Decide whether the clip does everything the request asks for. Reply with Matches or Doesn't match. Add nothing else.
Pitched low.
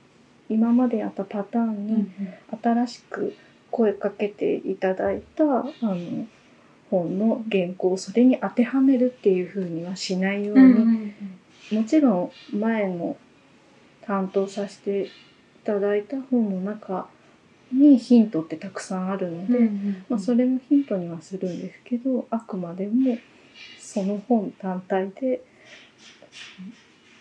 Doesn't match